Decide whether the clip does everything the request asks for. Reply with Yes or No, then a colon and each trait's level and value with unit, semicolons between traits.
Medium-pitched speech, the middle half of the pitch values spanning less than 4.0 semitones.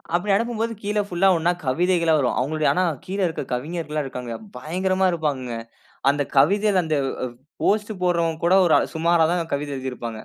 No: medium, 165 Hz; average, 4.4 semitones